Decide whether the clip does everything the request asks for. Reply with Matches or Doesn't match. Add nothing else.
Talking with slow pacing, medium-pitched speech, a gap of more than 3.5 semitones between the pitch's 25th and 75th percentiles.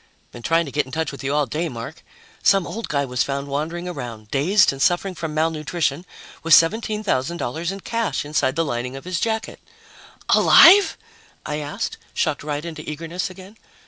Doesn't match